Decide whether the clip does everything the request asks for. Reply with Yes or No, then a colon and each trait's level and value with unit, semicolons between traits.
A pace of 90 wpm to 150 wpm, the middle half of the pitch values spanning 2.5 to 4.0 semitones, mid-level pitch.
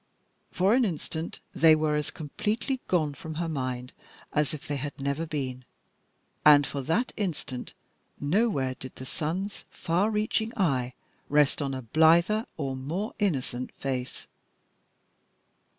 No: slow, 135 wpm; average, 5.2 semitones; medium, 150 Hz